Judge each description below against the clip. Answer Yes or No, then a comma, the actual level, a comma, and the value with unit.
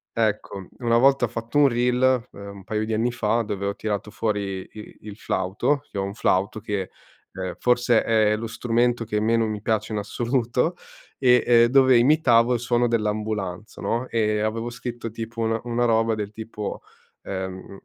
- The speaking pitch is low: Yes, low, 115 Hz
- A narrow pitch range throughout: Yes, narrow, 2.3 semitones